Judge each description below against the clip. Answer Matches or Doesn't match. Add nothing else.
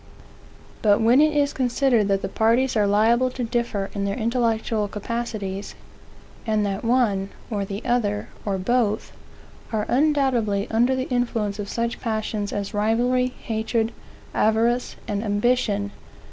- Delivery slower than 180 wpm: Matches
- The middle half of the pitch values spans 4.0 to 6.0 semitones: Doesn't match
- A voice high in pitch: Matches